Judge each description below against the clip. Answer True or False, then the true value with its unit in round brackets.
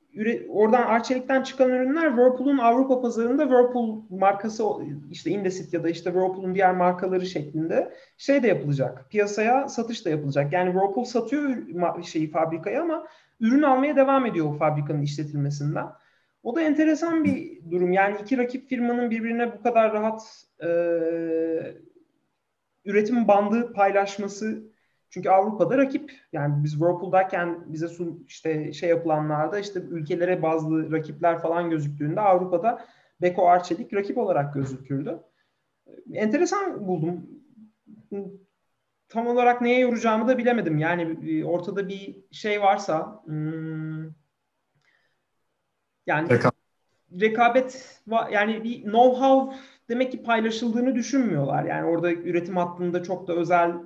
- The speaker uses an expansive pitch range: True (6.3 semitones)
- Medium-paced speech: True (120 wpm)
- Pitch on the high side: True (200 Hz)